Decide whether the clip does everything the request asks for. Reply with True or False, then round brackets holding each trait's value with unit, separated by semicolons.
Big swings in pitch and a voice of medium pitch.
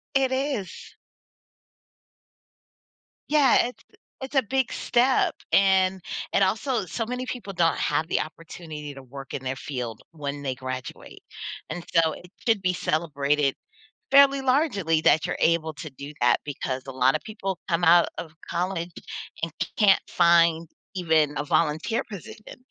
True (6.1 semitones; 170 Hz)